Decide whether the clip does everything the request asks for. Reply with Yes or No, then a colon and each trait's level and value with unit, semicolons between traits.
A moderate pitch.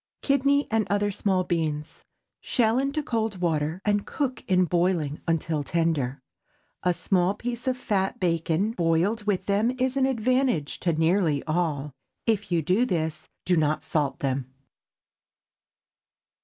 Yes: medium, 180 Hz